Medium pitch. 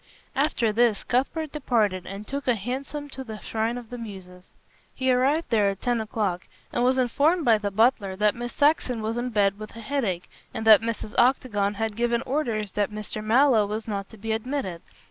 No: high, 225 Hz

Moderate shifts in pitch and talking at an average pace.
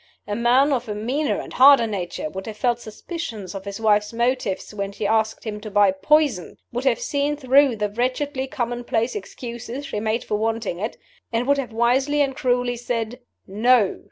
Yes: average, 3.7 semitones; average, 185 wpm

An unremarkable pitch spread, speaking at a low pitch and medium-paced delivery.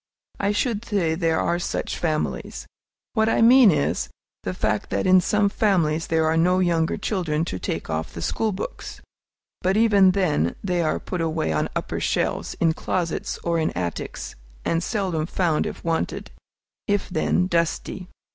No: average, 3.6 semitones; medium, 170 Hz; average, 165 wpm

